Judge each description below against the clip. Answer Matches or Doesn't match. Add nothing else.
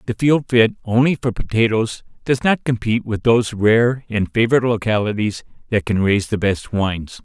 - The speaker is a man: Matches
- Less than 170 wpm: Doesn't match